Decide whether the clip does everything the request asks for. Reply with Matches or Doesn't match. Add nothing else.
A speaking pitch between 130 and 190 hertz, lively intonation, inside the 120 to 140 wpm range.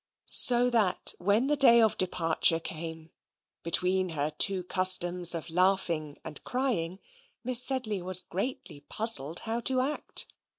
Matches